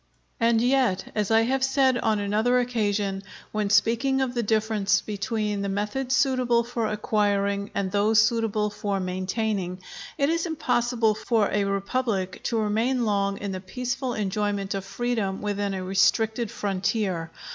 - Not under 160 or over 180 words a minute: No, average, 150 wpm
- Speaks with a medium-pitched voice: No, high, 215 Hz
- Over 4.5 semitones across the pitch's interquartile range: No, average, 3.1 semitones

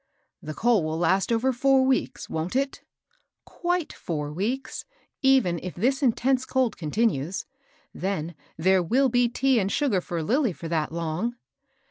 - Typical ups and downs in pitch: No, wide, 7.5 semitones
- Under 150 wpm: No, average, 155 wpm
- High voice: Yes, high, 225 Hz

